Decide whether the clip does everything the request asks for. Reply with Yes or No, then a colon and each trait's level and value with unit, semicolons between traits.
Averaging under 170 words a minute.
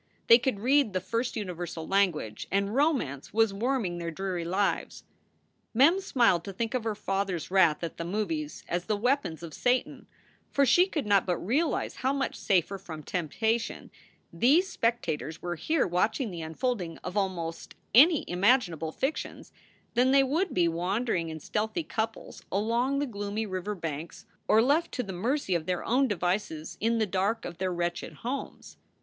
No: average, 180 wpm